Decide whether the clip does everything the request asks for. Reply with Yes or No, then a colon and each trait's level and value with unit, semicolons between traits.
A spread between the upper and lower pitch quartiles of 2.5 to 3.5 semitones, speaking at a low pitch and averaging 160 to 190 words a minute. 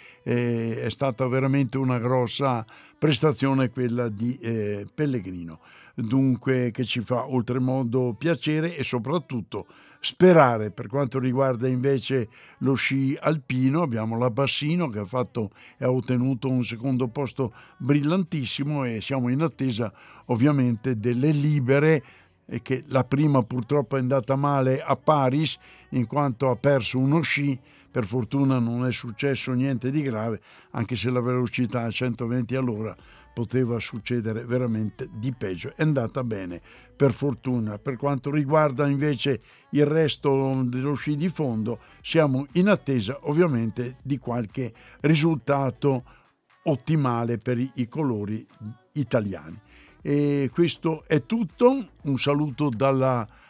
No: average, 2.8 semitones; low, 130 Hz; average, 130 wpm